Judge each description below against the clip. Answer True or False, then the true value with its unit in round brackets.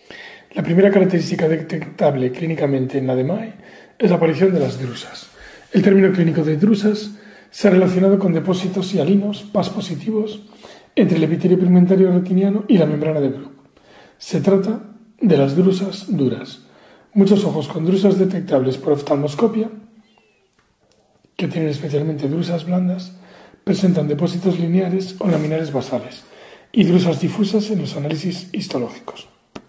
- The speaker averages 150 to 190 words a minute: False (135 wpm)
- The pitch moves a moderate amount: True (3.9 semitones)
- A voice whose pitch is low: False (185 Hz)